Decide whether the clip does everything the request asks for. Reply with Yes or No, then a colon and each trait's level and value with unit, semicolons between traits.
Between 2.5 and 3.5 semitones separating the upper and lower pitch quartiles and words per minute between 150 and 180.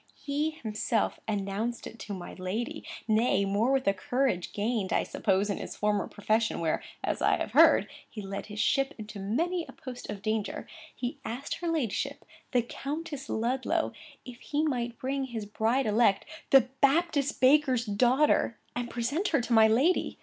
No: average, 4.6 semitones; average, 175 wpm